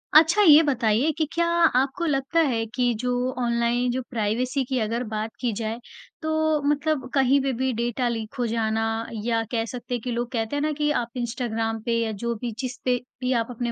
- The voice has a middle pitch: No, high, 245 Hz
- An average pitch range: Yes, average, 3.0 semitones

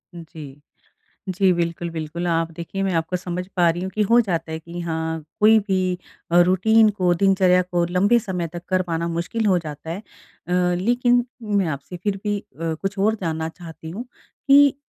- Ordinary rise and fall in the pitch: Yes, average, 3.0 semitones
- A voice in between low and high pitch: Yes, medium, 180 Hz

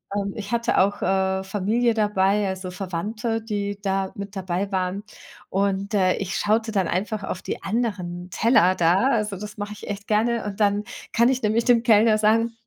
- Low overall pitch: No, high, 205 Hz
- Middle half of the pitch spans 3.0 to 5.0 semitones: No, narrow, 2.4 semitones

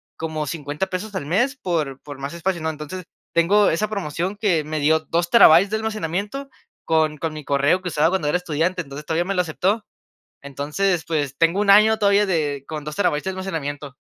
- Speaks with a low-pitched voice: No, medium, 165 Hz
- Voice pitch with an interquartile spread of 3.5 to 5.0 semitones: Yes, average, 4.3 semitones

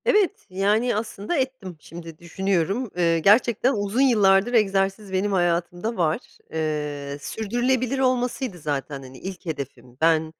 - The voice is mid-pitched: No, high, 195 Hz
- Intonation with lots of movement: Yes, wide, 6.2 semitones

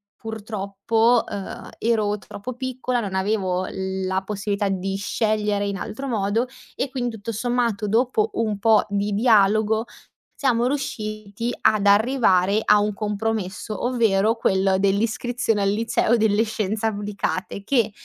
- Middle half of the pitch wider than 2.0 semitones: Yes, narrow, 2.4 semitones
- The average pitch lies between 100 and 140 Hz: No, high, 215 Hz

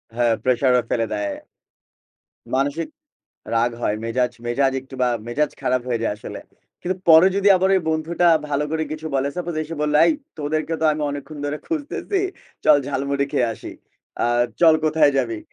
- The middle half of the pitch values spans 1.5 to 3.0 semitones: No, average, 4.3 semitones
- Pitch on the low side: No, medium, 145 Hz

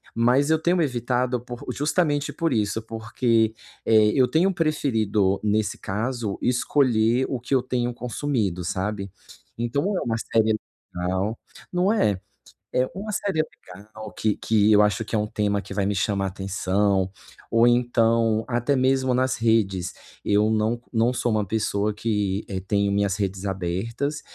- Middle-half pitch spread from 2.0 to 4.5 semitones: Yes, average, 3.6 semitones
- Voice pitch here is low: Yes, low, 110 Hz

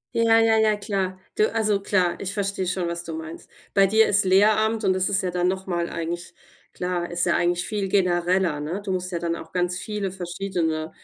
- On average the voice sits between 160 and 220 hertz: Yes, medium, 185 Hz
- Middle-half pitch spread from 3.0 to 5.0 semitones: No, narrow, 2.5 semitones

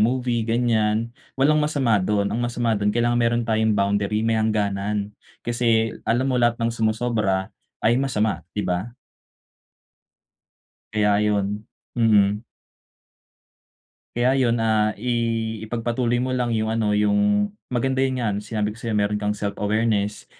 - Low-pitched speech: Yes, low, 110 Hz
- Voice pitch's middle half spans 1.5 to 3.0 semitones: Yes, narrow, 2.4 semitones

